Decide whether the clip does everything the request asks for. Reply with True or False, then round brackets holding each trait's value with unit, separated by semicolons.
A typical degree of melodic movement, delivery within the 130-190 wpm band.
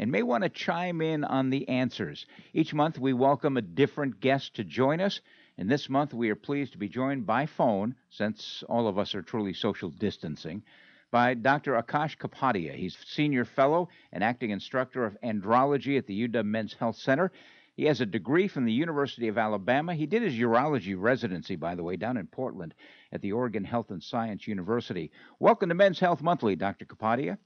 False (4.5 semitones; 200 wpm)